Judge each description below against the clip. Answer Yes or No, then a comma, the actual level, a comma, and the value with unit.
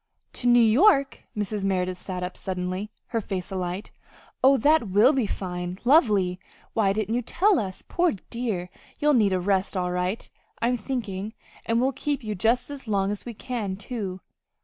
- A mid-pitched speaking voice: No, high, 210 Hz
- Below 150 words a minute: No, average, 175 wpm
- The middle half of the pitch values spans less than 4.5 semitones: No, average, 4.8 semitones